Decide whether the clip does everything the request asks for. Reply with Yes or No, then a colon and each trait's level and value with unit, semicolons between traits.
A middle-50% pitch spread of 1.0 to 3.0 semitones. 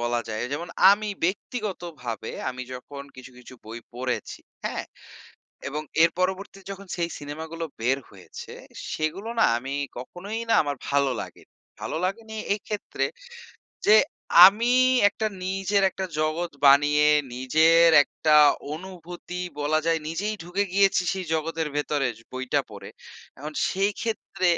No: average, 5.3 semitones